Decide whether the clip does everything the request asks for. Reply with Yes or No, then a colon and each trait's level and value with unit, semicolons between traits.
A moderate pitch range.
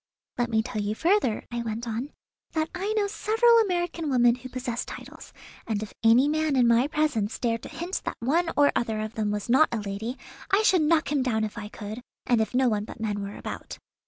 No: wide, 6.1 semitones